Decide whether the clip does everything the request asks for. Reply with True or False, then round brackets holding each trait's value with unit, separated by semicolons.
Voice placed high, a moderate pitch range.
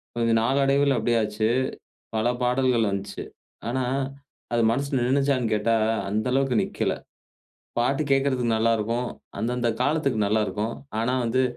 False (120 Hz; 3.1 semitones)